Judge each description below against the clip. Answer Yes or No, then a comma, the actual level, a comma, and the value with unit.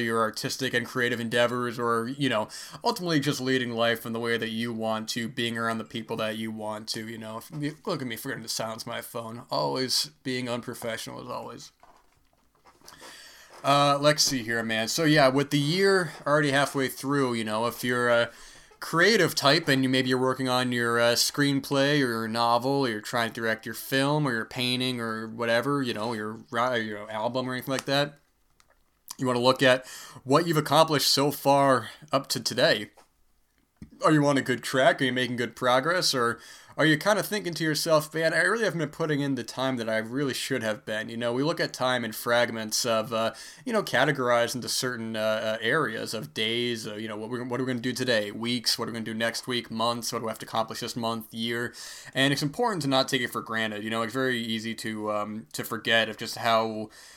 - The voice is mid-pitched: No, low, 120 Hz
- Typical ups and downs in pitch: Yes, average, 3.3 semitones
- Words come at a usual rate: No, fast, 225 wpm